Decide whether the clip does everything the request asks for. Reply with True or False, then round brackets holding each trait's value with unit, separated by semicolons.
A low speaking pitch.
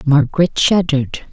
False (150 Hz)